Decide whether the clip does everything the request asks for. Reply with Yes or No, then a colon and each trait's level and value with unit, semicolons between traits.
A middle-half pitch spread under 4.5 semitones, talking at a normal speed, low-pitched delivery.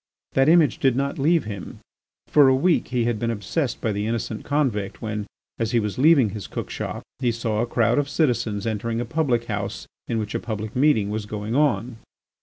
No: average, 4.0 semitones; fast, 210 wpm; low, 115 Hz